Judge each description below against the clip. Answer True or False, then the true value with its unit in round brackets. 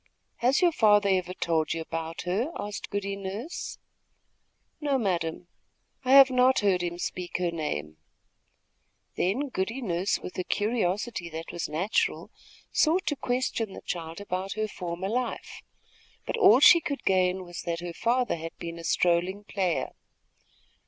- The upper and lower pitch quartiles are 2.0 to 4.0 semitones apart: False (5.6 semitones)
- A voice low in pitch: False (190 Hz)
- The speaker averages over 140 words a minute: True (150 wpm)